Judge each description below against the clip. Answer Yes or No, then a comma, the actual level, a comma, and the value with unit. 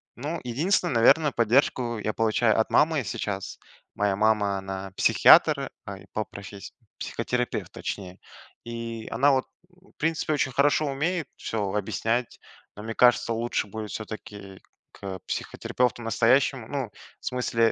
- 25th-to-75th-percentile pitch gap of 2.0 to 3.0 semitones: No, average, 4.3 semitones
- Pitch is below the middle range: Yes, low, 115 Hz